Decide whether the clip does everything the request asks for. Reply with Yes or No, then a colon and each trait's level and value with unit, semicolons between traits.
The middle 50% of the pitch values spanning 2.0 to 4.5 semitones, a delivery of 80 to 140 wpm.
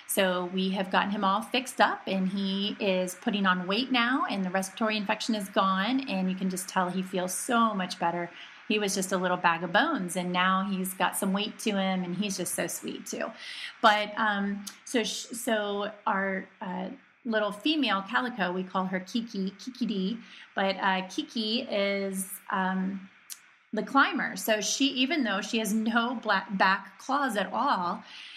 No: average, 3.0 semitones; average, 185 wpm